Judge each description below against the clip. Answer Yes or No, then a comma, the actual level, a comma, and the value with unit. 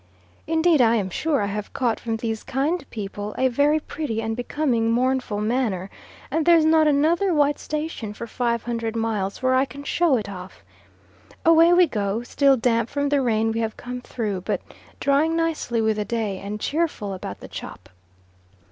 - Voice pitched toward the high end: Yes, high, 245 Hz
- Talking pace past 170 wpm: Yes, average, 180 wpm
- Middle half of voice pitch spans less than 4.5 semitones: No, average, 5.1 semitones